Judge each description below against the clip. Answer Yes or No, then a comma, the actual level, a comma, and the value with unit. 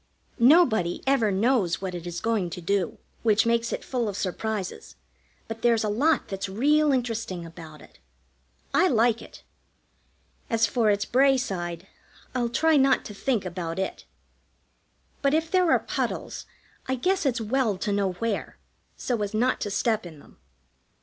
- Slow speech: No, average, 165 wpm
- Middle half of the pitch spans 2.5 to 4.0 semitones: No, average, 5.1 semitones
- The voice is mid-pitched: No, high, 225 Hz